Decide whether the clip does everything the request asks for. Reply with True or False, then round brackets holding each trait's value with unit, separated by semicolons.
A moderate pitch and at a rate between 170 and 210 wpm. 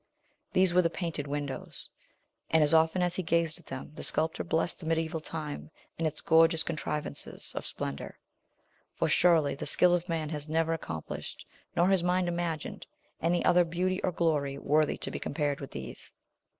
True (160 Hz; 175 wpm)